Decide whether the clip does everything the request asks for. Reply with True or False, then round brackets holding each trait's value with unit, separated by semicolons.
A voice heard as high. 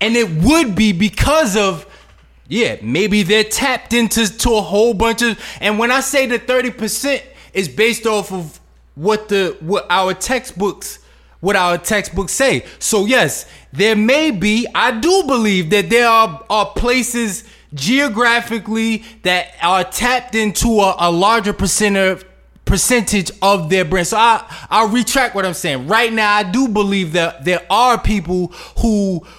True (215 Hz)